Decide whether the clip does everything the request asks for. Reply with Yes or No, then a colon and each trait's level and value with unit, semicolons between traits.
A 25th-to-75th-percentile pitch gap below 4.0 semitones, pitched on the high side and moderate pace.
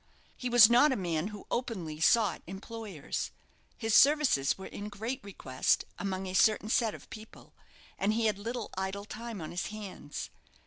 Yes: average, 3.3 semitones; high, 210 Hz; average, 170 wpm